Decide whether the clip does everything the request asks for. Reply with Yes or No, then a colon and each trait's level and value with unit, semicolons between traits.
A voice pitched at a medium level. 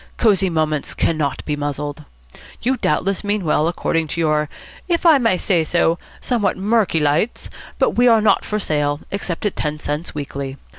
Yes: medium, 165 Hz